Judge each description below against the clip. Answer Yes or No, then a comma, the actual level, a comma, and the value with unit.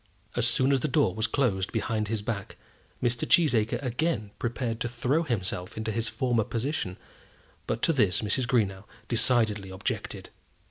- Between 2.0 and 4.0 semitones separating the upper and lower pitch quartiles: Yes, average, 3.3 semitones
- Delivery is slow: No, average, 155 wpm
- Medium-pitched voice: No, low, 115 Hz